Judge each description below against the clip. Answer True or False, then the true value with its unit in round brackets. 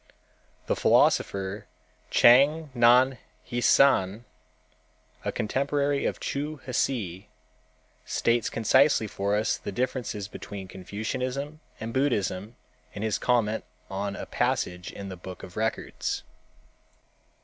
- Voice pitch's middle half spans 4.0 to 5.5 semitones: True (4.8 semitones)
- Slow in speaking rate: True (105 wpm)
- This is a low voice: True (115 Hz)